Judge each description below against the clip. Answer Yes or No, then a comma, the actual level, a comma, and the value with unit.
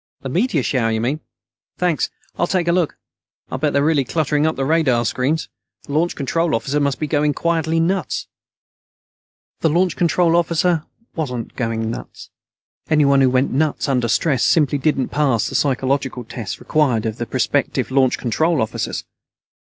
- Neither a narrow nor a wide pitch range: Yes, average, 4.0 semitones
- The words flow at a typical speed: Yes, average, 160 wpm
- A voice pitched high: No, medium, 145 Hz